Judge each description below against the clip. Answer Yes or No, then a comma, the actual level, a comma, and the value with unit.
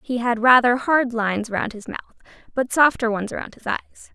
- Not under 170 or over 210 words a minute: Yes, fast, 205 wpm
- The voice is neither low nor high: No, high, 240 Hz